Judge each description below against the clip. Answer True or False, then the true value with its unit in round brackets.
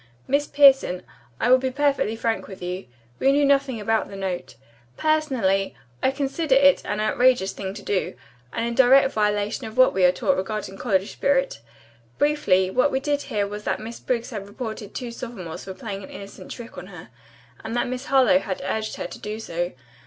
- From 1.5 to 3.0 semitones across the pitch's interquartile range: False (5.4 semitones)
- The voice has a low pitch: False (225 Hz)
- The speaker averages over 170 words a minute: True (195 wpm)